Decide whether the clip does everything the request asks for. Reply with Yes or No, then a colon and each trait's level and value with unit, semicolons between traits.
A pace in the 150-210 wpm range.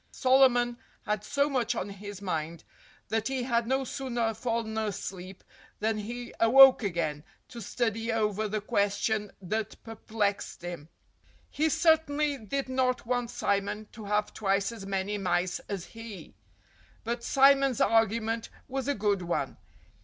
No: average, 140 wpm